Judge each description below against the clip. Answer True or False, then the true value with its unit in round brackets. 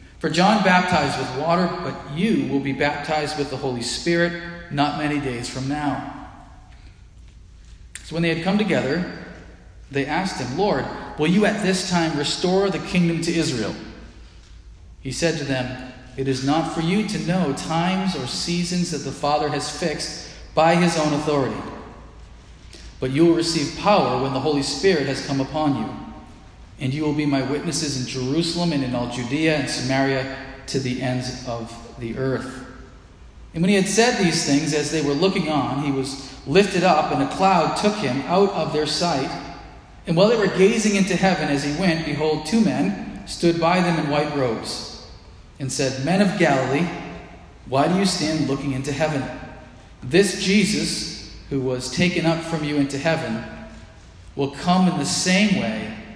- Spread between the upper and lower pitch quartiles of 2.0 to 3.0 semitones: False (4.6 semitones)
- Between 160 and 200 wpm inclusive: True (180 wpm)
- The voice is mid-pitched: True (150 Hz)